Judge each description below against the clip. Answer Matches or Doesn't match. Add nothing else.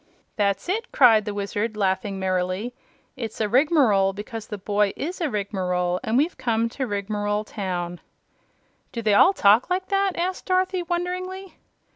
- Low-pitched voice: Doesn't match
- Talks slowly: Doesn't match